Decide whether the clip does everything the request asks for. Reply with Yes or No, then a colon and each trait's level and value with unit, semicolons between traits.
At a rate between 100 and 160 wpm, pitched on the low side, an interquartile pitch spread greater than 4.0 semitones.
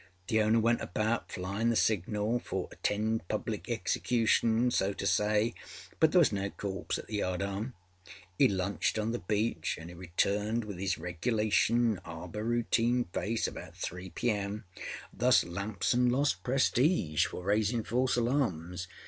No: average, 150 wpm; low, 105 Hz; average, 3.6 semitones